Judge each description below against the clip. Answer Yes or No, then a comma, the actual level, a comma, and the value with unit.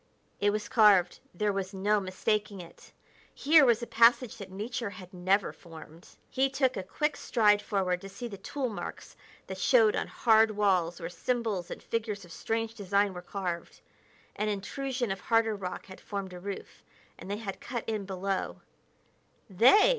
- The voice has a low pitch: No, high, 205 Hz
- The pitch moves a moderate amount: Yes, average, 3.4 semitones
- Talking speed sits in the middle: Yes, average, 175 wpm